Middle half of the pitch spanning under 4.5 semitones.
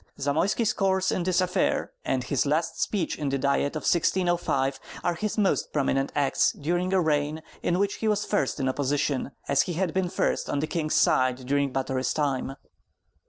No: average, 4.8 semitones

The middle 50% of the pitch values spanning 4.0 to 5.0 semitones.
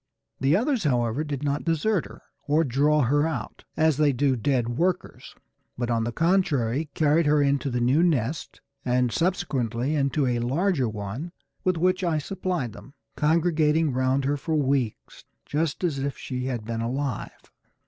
Yes: average, 4.3 semitones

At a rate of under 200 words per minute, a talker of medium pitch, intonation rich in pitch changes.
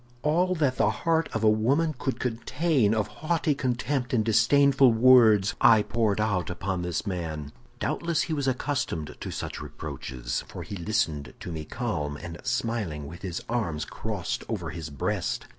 No: average, 165 wpm; low, 110 Hz; wide, 7.3 semitones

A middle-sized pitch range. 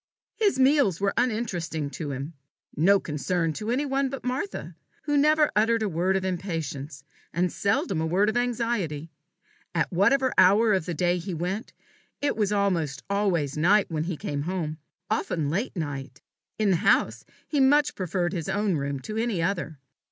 No: wide, 5.9 semitones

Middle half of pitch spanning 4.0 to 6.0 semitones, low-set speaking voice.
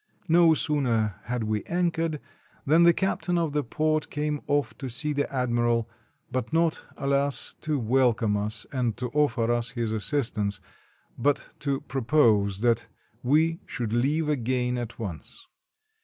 Yes: average, 4.5 semitones; low, 130 Hz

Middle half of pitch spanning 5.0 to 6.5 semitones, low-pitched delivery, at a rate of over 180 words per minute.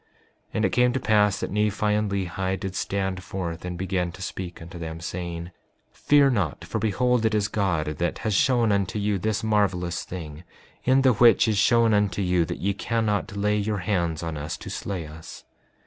No: average, 3.5 semitones; low, 100 Hz; average, 200 wpm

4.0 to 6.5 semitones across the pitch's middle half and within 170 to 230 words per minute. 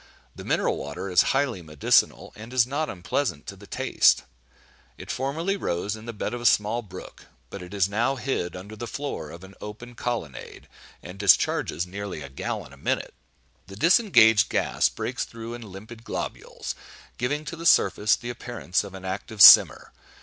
Yes: average, 4.4 semitones; average, 180 wpm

